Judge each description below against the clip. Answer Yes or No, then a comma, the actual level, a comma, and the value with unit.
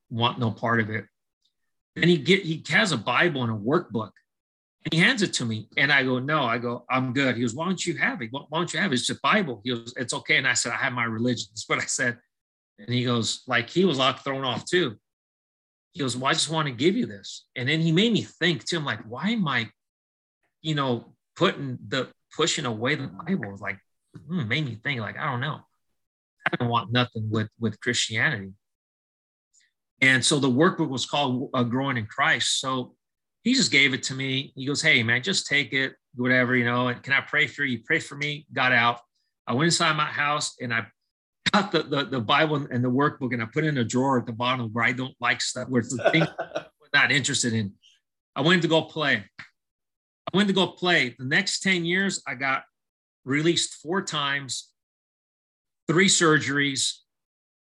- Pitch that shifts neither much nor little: Yes, average, 4.7 semitones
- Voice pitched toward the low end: Yes, low, 130 Hz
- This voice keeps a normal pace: No, fast, 225 wpm